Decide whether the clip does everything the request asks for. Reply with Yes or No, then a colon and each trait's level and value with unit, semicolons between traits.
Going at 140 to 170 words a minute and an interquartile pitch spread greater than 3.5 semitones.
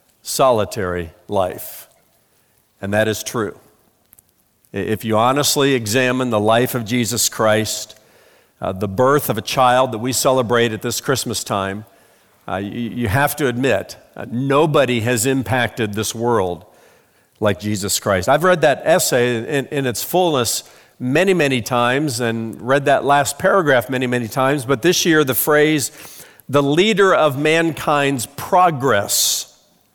Yes: average, 145 wpm; average, 4.4 semitones